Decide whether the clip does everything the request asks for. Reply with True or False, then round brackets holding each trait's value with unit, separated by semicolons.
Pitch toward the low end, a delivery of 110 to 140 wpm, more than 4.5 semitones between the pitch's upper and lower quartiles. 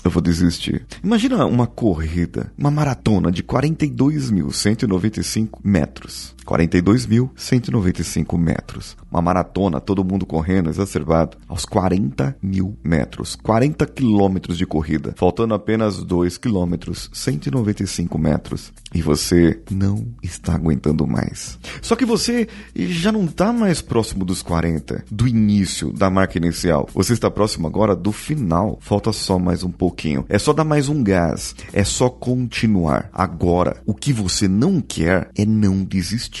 True (100 Hz; 135 wpm; 5.4 semitones)